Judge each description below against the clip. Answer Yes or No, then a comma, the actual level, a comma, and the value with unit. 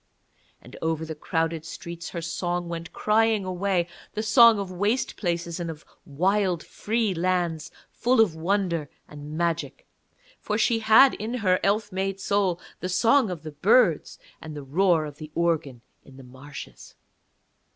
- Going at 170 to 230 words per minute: No, average, 160 wpm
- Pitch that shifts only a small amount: No, average, 4.1 semitones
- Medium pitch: Yes, medium, 175 Hz